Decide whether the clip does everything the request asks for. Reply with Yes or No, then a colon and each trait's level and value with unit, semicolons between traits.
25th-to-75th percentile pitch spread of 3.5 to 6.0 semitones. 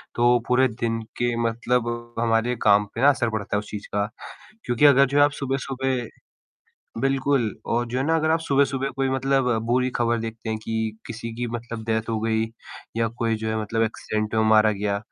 No: average, 3.0 semitones